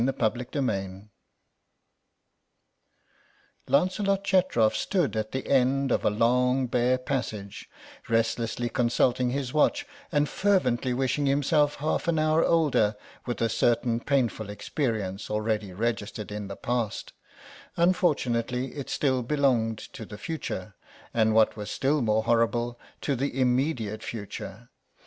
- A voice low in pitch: Yes, low, 125 Hz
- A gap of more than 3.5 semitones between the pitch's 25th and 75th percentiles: Yes, average, 4.1 semitones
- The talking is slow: Yes, slow, 125 wpm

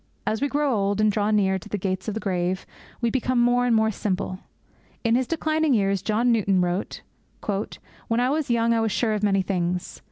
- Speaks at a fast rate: Yes, fast, 215 wpm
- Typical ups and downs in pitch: Yes, average, 3.7 semitones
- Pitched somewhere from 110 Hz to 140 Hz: No, high, 215 Hz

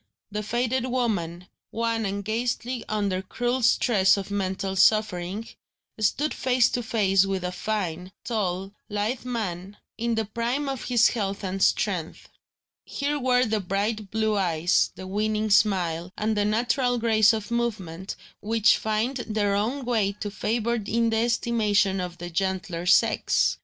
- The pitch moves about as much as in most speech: Yes, average, 3.4 semitones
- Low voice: No, high, 215 Hz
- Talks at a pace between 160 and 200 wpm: No, average, 150 wpm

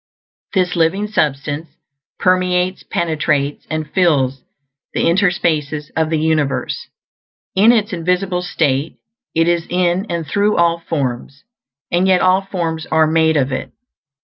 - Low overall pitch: No, medium, 165 Hz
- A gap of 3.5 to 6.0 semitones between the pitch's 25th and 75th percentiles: No, average, 3.0 semitones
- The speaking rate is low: Yes, slow, 130 wpm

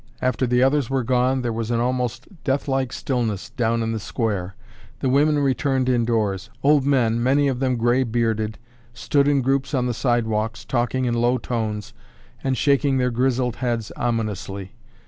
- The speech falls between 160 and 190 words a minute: Yes, average, 165 wpm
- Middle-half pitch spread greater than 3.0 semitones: No, narrow, 2.6 semitones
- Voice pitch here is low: Yes, low, 125 Hz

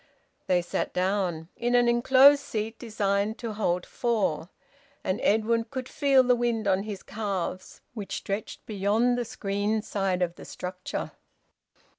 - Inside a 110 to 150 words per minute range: Yes, average, 145 wpm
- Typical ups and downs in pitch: Yes, average, 3.7 semitones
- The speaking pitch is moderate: No, high, 210 Hz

